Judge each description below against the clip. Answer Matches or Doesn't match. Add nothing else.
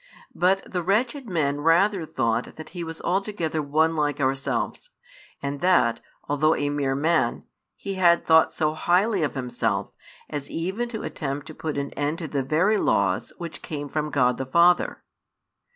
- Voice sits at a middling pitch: Matches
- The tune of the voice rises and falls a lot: Doesn't match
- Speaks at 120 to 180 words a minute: Matches